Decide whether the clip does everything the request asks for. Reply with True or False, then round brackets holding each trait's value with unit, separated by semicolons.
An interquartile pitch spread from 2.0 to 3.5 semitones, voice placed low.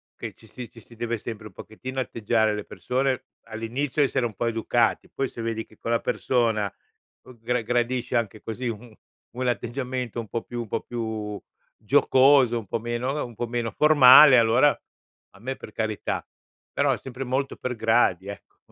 True (2.4 semitones; 120 Hz)